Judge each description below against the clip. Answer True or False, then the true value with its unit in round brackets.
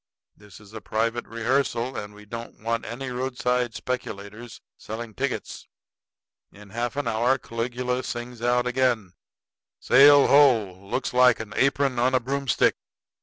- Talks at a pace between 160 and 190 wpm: False (140 wpm)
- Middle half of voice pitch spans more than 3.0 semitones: False (2.4 semitones)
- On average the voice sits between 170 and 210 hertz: False (120 Hz)